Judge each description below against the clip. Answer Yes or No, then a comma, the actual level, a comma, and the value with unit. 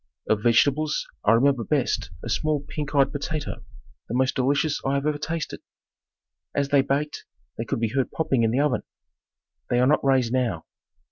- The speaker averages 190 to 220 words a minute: No, average, 180 wpm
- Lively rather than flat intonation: No, average, 3.1 semitones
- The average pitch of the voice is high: No, medium, 140 Hz